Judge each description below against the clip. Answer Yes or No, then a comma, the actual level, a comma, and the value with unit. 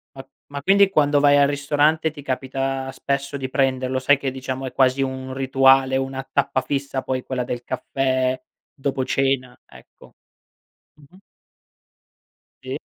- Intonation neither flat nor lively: No, narrow, 1.4 semitones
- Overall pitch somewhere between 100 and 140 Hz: Yes, low, 135 Hz